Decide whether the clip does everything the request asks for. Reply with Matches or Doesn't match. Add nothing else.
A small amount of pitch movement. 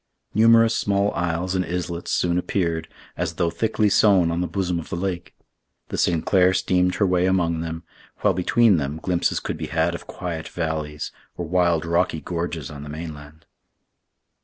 Matches